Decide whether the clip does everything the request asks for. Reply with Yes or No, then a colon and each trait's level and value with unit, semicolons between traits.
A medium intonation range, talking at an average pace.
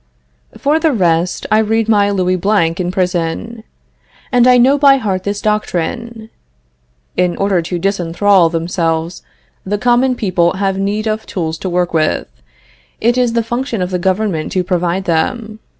Yes: average, 4.2 semitones; average, 160 wpm